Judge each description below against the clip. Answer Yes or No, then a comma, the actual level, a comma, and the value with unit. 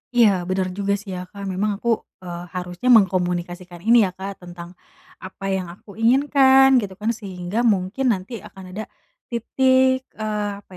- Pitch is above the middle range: Yes, high, 195 Hz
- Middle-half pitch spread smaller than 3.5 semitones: No, average, 4.4 semitones